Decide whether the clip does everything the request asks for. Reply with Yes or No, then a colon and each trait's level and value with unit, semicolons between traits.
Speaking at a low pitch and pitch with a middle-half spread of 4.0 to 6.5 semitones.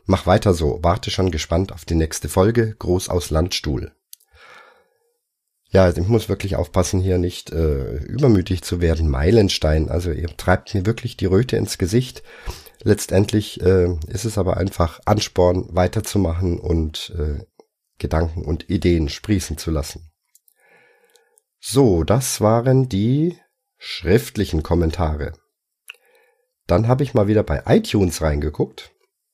Yes: very low, 95 Hz; average, 4.8 semitones